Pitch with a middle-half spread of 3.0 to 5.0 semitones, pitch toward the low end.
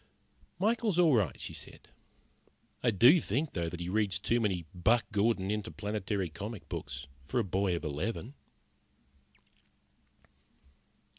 Yes: average, 4.7 semitones; low, 105 Hz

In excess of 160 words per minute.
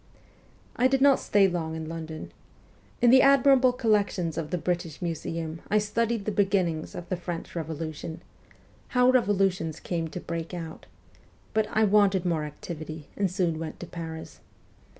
No: average, 155 wpm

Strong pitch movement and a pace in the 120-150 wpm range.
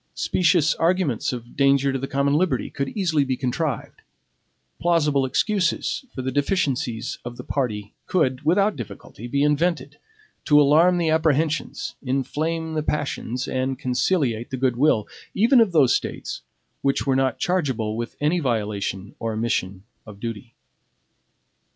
No: average, 4.8 semitones; average, 145 wpm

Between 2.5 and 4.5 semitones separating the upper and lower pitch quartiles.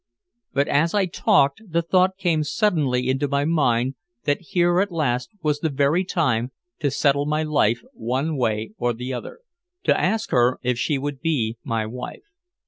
No: average, 4.9 semitones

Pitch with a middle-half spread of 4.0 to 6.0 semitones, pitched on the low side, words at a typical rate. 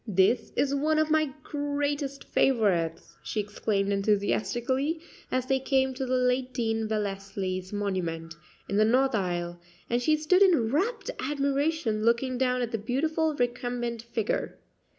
No: average, 5.1 semitones; high, 245 Hz; average, 145 wpm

